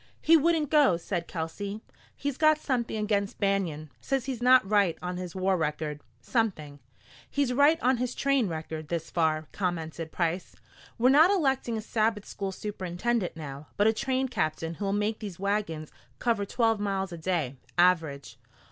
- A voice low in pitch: No, high, 200 Hz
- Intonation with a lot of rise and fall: Yes, wide, 6.6 semitones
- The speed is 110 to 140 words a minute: No, average, 165 wpm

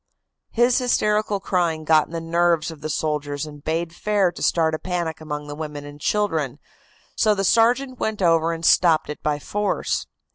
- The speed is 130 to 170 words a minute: No, average, 185 wpm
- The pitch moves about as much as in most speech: Yes, average, 4.8 semitones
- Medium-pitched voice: Yes, medium, 165 Hz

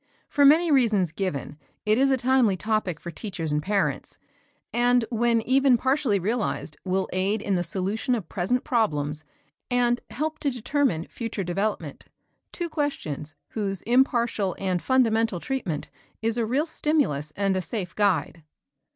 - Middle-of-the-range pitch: No, high, 215 Hz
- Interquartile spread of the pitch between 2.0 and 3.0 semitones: No, wide, 5.5 semitones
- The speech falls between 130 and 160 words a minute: Yes, average, 150 wpm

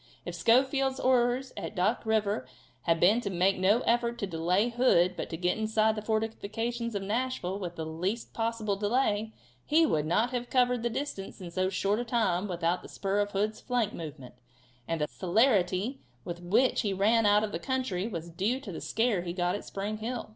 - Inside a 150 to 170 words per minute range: No, average, 200 wpm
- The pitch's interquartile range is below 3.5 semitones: No, average, 4.5 semitones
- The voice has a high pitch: Yes, high, 210 Hz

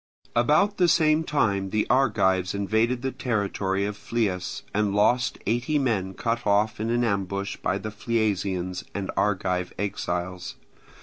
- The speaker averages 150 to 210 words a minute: No, average, 140 wpm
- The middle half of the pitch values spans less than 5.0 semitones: Yes, average, 3.6 semitones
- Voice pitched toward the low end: Yes, low, 105 Hz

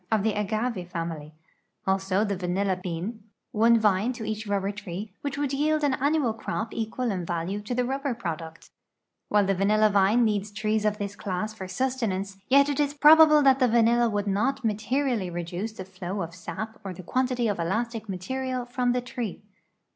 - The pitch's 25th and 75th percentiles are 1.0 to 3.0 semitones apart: No, average, 4.4 semitones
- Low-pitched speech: No, high, 215 Hz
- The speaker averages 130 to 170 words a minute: No, average, 185 wpm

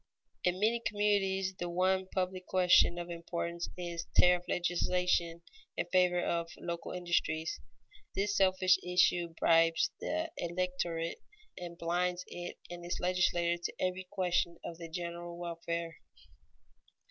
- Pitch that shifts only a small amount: Yes, narrow, 1.2 semitones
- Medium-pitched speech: Yes, medium, 175 Hz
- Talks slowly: Yes, slow, 130 wpm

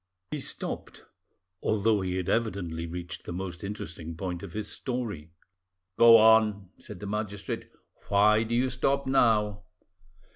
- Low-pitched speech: Yes, low, 105 Hz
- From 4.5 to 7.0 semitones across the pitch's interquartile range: No, average, 3.8 semitones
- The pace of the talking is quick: No, average, 140 wpm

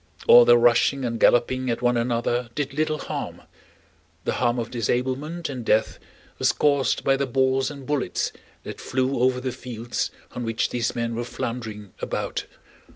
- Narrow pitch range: Yes, narrow, 2.1 semitones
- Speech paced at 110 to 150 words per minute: No, average, 165 wpm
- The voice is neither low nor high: No, low, 125 Hz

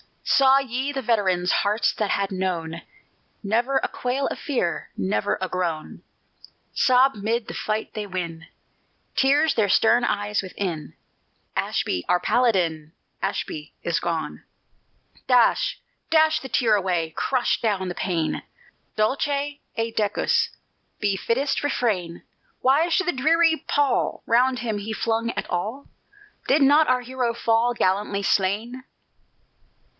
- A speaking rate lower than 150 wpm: Yes, slow, 135 wpm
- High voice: Yes, high, 225 Hz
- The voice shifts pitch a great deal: Yes, wide, 5.9 semitones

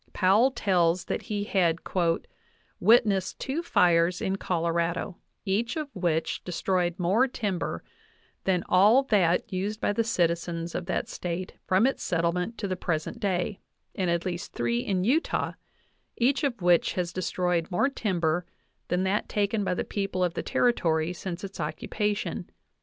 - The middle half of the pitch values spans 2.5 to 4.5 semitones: Yes, average, 3.3 semitones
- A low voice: No, medium, 185 Hz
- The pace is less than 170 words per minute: Yes, average, 150 wpm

